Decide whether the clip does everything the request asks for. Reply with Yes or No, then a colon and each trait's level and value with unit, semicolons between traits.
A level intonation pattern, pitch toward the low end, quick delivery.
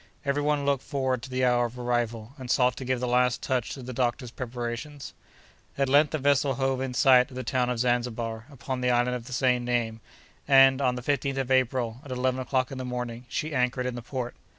Yes: narrow, 1.5 semitones; low, 125 Hz; fast, 230 wpm